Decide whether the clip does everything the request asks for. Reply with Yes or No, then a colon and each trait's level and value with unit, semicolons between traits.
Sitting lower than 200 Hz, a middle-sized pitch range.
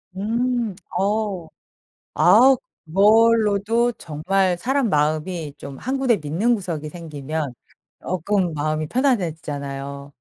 No: medium, 185 Hz; wide, 6.6 semitones